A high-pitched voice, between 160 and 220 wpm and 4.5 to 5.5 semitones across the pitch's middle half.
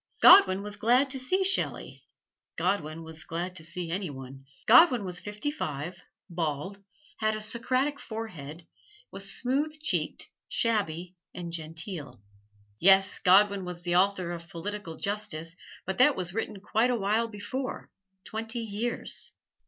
No: high, 195 Hz; average, 140 wpm; average, 4.8 semitones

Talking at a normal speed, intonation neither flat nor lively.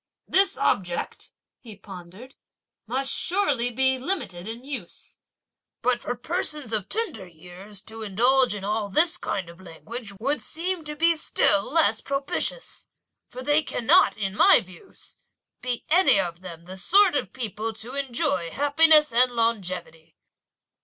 No: average, 145 wpm; wide, 7.0 semitones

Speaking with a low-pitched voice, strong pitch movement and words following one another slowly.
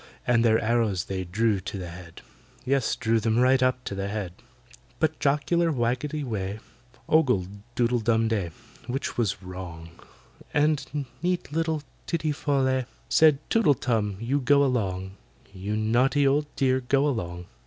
No: low, 120 Hz; wide, 5.7 semitones; average, 155 wpm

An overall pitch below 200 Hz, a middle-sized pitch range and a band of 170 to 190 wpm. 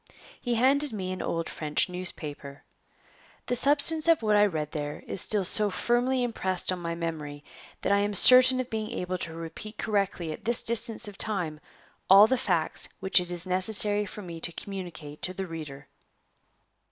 Yes: high, 190 Hz; average, 4.9 semitones; average, 180 wpm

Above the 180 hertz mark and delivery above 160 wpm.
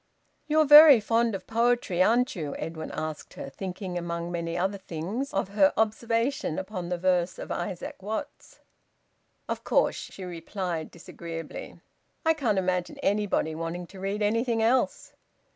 No: high, 190 Hz; average, 145 wpm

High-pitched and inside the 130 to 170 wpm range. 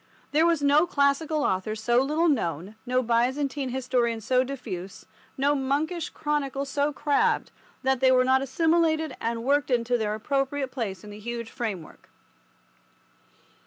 Yes: very high, 265 Hz; average, 145 wpm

